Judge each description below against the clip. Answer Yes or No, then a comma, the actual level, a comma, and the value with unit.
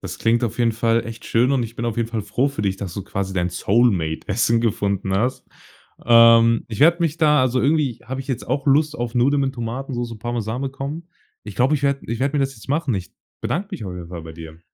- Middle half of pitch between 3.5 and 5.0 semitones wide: Yes, average, 4.3 semitones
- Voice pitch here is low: Yes, low, 120 Hz